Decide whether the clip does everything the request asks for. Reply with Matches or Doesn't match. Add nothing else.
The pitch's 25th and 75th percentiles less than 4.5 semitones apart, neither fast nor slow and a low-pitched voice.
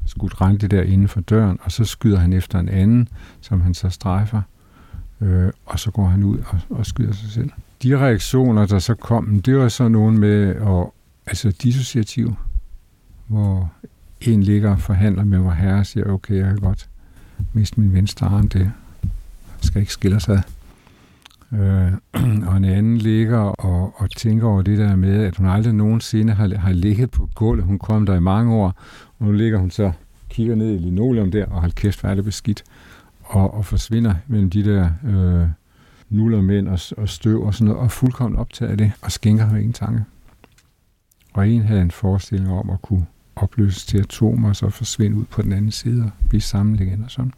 Matches